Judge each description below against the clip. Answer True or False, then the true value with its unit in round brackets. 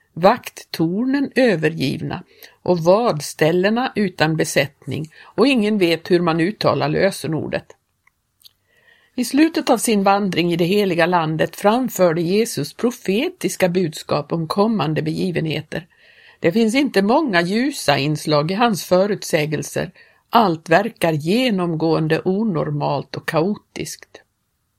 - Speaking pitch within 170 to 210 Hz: True (185 Hz)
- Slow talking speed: True (105 wpm)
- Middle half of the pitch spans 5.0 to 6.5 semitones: True (5.6 semitones)